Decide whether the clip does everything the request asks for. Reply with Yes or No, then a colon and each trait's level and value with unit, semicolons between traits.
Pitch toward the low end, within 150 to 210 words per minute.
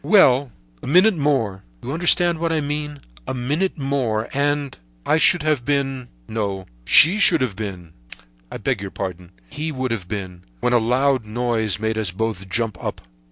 Yes: low, 120 Hz; average, 155 wpm